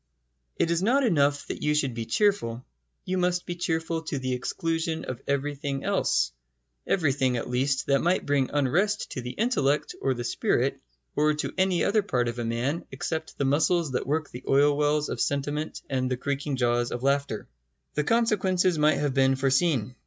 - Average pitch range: Yes, average, 4.1 semitones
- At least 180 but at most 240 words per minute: Yes, average, 185 wpm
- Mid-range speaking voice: Yes, medium, 145 Hz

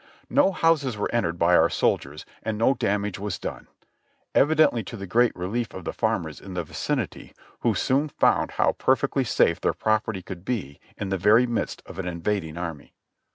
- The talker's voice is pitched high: No, low, 105 Hz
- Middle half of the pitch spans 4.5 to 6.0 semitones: Yes, average, 5.1 semitones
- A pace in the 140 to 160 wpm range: No, average, 185 wpm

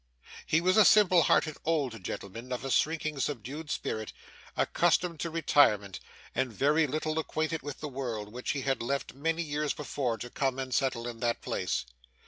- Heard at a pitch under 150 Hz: Yes, medium, 140 Hz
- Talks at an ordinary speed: Yes, average, 175 wpm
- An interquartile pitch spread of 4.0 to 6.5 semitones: Yes, average, 4.4 semitones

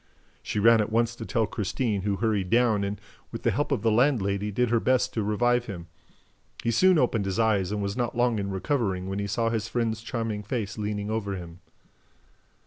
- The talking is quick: Yes, fast, 210 wpm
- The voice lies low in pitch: Yes, low, 110 Hz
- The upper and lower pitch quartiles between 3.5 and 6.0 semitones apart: No, average, 2.8 semitones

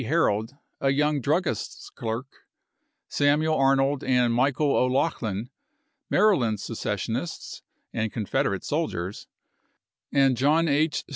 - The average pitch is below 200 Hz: Yes, low, 135 Hz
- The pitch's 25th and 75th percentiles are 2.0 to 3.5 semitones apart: No, average, 4.2 semitones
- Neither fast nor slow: No, slow, 100 wpm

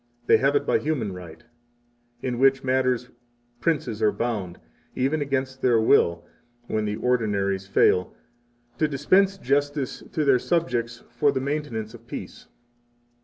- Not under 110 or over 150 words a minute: Yes, average, 140 wpm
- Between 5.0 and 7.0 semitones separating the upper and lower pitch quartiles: No, average, 4.4 semitones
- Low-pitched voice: Yes, low, 125 Hz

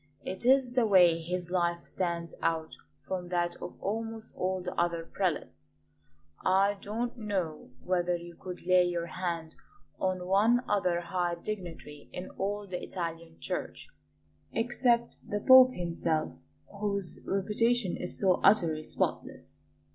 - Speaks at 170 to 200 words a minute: No, slow, 135 wpm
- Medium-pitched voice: Yes, medium, 180 Hz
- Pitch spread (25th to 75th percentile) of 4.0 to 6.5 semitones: No, average, 3.2 semitones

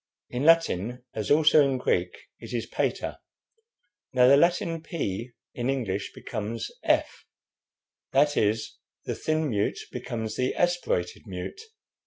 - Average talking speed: No, slow, 130 wpm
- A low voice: Yes, low, 125 Hz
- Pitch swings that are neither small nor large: No, wide, 6.2 semitones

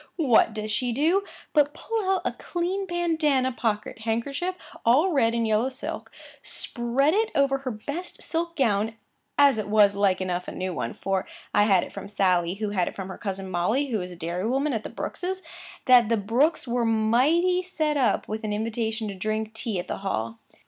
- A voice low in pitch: No, high, 230 Hz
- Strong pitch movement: Yes, wide, 5.9 semitones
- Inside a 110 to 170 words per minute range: No, average, 195 wpm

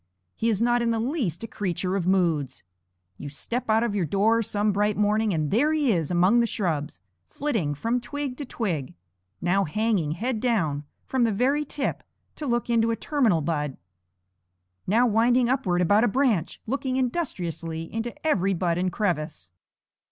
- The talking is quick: No, average, 175 wpm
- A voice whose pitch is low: No, high, 210 Hz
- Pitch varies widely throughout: Yes, wide, 5.8 semitones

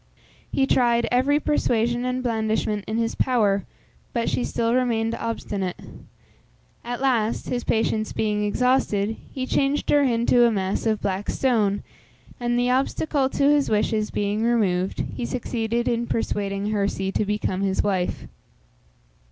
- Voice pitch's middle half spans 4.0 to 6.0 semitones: No, average, 3.1 semitones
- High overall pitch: Yes, high, 230 Hz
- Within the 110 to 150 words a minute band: Yes, average, 145 wpm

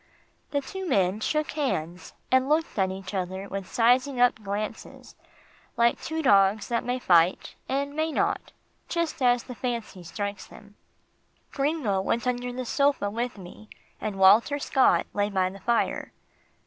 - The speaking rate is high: No, average, 155 wpm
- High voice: Yes, high, 235 Hz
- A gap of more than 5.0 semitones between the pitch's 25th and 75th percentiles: Yes, wide, 5.4 semitones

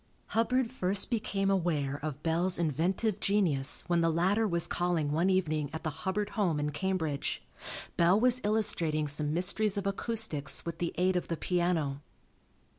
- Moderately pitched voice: Yes, medium, 175 Hz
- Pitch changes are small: No, average, 4.2 semitones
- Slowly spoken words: No, average, 160 wpm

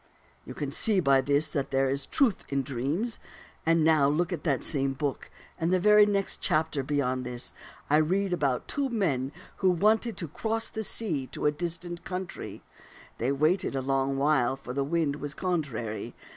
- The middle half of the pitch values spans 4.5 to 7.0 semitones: Yes, average, 5.0 semitones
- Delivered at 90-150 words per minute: No, average, 185 wpm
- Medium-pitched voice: Yes, medium, 150 Hz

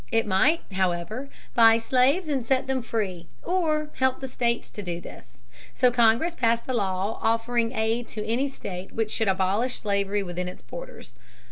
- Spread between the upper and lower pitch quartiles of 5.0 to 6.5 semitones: No, average, 4.6 semitones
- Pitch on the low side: No, high, 230 Hz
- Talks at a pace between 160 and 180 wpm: Yes, average, 170 wpm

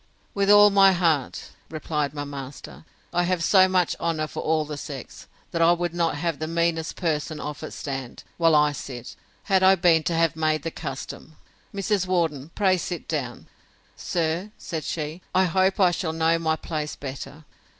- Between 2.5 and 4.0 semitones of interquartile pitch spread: Yes, average, 2.8 semitones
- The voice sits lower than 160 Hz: No, medium, 165 Hz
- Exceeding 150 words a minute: Yes, average, 180 wpm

